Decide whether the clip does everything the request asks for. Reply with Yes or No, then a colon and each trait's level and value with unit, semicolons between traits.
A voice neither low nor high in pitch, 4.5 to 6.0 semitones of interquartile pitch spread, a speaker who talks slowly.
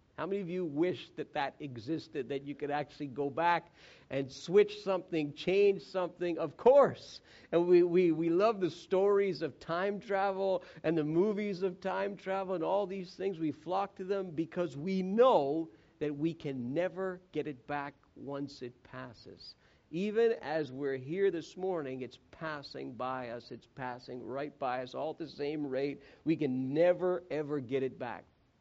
No: medium, 165 Hz; average, 4.8 semitones; average, 180 wpm